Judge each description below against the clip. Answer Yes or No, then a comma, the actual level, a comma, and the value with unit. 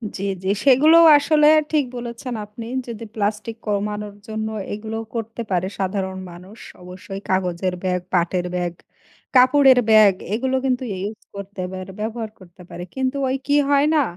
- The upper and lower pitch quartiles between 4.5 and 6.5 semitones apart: Yes, average, 4.9 semitones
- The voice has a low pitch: No, high, 215 Hz